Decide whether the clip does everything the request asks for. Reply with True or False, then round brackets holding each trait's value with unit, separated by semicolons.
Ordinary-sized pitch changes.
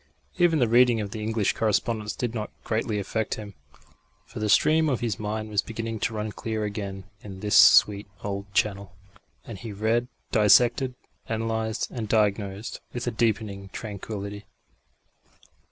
False (2.0 semitones)